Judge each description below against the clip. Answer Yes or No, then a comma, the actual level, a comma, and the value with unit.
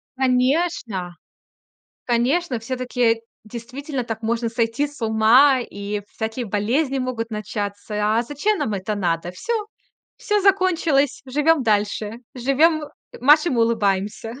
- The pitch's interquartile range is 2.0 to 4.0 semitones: No, average, 4.5 semitones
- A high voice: Yes, high, 240 Hz